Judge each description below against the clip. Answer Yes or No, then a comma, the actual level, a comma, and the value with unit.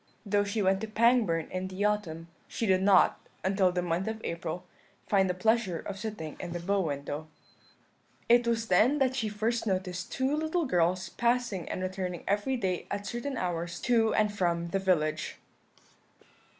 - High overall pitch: Yes, high, 195 Hz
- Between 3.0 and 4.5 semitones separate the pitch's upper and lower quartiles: Yes, average, 4.0 semitones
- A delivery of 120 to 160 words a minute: No, average, 175 wpm